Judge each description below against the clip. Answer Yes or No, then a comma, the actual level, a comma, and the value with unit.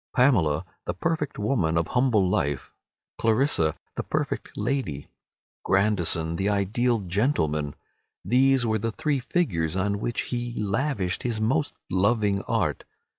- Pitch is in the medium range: No, low, 105 Hz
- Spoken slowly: Yes, slow, 125 wpm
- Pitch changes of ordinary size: No, wide, 5.9 semitones